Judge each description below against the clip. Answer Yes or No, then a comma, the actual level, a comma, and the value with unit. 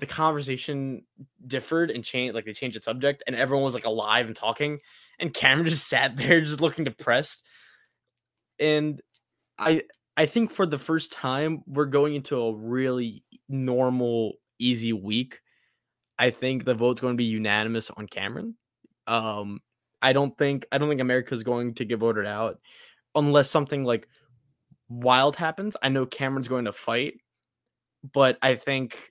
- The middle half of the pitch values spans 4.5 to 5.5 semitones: No, average, 3.4 semitones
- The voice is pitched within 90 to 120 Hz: No, low, 130 Hz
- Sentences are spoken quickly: No, average, 160 wpm